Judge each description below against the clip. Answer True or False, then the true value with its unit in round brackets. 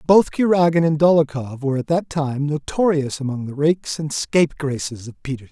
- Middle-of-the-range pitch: True (150 Hz)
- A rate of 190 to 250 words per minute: False (175 wpm)